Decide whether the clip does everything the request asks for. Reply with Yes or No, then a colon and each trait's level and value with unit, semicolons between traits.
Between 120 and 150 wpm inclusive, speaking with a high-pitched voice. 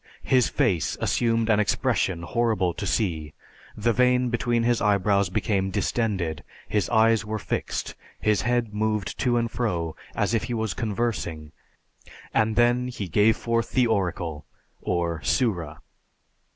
No: average, 140 wpm; low, 110 Hz